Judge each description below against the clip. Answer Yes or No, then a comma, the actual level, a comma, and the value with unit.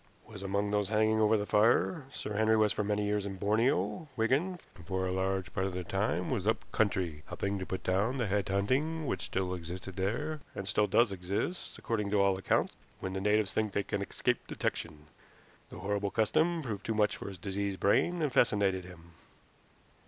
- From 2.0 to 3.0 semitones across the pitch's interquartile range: Yes, narrow, 2.6 semitones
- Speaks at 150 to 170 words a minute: No, average, 200 wpm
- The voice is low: Yes, low, 100 Hz